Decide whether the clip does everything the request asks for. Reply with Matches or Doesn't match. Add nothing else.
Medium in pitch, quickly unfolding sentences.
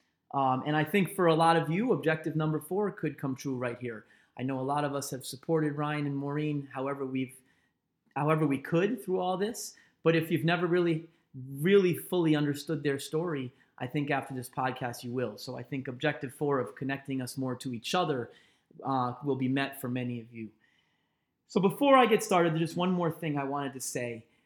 Matches